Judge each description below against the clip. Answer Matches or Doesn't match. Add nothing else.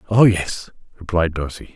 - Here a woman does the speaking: Doesn't match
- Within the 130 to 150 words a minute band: Matches